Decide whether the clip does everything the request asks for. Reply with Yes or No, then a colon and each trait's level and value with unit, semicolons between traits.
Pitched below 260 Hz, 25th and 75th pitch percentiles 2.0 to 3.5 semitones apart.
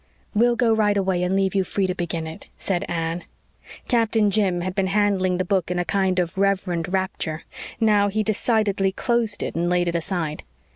Yes: high, 190 Hz; average, 2.7 semitones